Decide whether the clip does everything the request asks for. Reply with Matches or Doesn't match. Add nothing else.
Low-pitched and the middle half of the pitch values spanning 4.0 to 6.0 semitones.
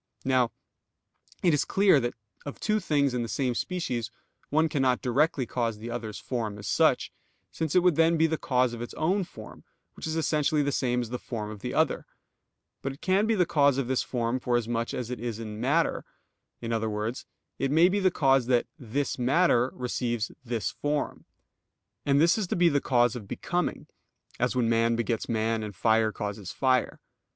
Matches